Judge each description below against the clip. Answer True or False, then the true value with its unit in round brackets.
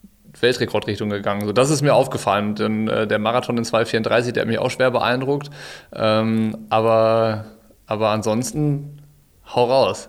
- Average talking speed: True (150 wpm)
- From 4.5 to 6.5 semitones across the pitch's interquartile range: False (2.7 semitones)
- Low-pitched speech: True (110 Hz)